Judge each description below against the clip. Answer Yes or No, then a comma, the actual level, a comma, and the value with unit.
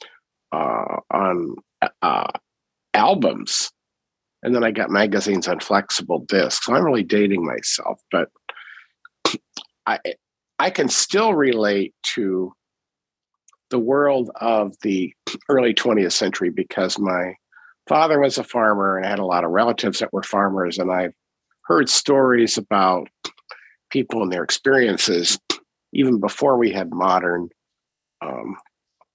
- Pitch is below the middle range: Yes, low, 105 Hz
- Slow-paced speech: Yes, slow, 130 wpm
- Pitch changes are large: Yes, wide, 6.3 semitones